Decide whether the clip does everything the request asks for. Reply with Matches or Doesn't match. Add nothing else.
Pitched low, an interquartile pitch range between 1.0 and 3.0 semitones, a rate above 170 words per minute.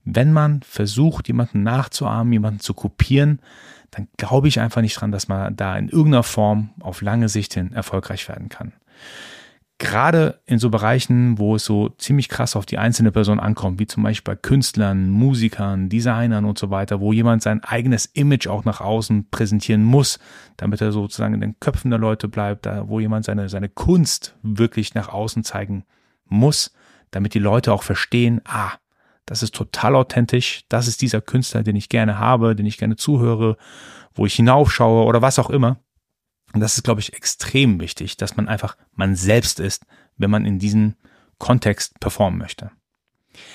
Matches